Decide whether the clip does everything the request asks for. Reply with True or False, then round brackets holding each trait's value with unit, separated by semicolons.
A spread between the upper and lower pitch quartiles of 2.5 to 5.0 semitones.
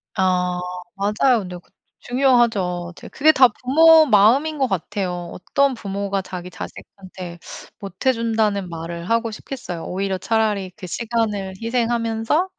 True (4.6 semitones)